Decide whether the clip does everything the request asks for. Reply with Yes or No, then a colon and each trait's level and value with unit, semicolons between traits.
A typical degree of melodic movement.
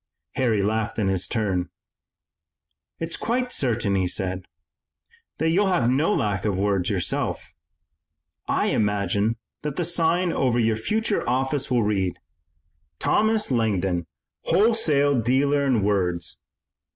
No: wide, 7.1 semitones